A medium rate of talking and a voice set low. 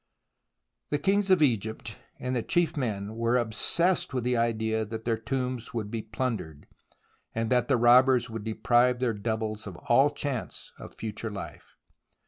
Yes: average, 160 wpm; low, 115 Hz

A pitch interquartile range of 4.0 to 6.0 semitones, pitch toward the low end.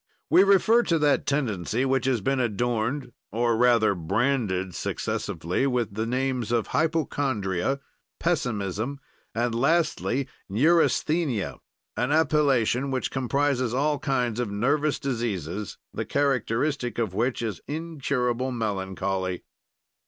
Yes: average, 4.4 semitones; low, 125 Hz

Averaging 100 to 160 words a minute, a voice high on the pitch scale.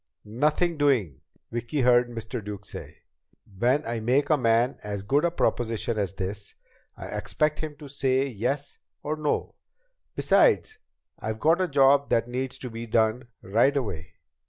No: average, 155 wpm; low, 125 Hz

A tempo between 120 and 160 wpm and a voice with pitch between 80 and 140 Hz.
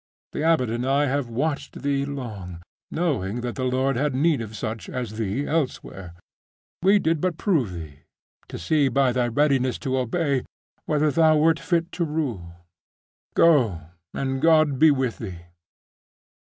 Yes: average, 155 wpm; low, 135 Hz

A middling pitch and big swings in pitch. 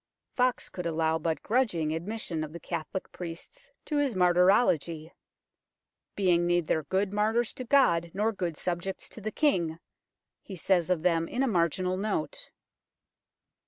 No: medium, 180 Hz; average, 4.2 semitones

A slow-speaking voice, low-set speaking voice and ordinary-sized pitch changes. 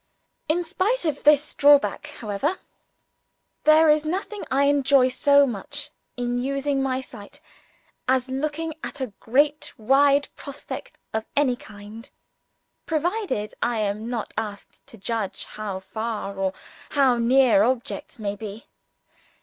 No: slow, 130 wpm; very high, 260 Hz; average, 4.9 semitones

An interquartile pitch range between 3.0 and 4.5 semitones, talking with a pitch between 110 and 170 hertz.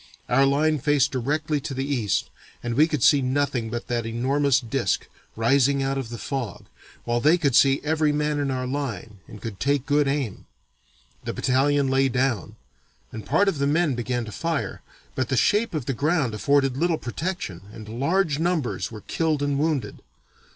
Yes: average, 3.5 semitones; low, 135 Hz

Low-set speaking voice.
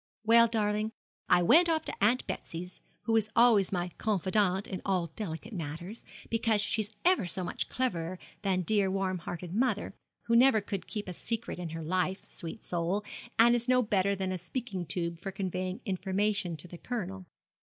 No: high, 195 Hz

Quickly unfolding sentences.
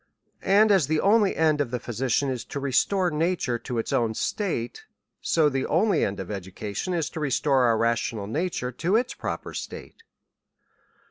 No: average, 175 wpm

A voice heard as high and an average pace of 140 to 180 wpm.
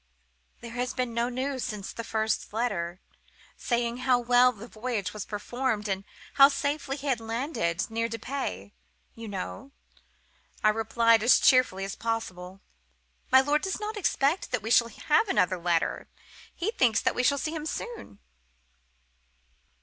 Yes: high, 235 Hz; average, 150 wpm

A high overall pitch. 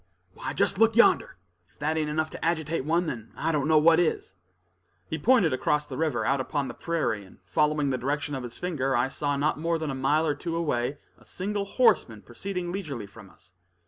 No: medium, 150 Hz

